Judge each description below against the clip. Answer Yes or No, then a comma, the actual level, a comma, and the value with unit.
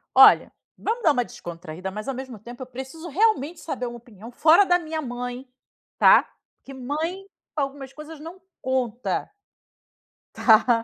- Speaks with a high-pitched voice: Yes, very high, 265 Hz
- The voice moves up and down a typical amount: Yes, average, 4.7 semitones